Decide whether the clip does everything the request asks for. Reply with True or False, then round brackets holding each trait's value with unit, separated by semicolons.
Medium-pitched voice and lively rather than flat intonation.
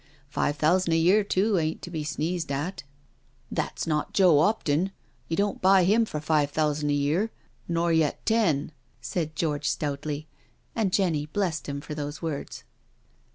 False (160 Hz; 3.8 semitones)